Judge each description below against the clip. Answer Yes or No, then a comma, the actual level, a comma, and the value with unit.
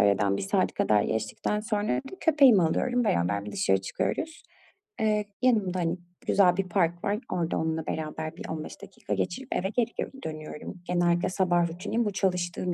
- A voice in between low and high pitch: Yes, medium, 175 Hz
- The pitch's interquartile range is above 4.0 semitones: Yes, average, 5.0 semitones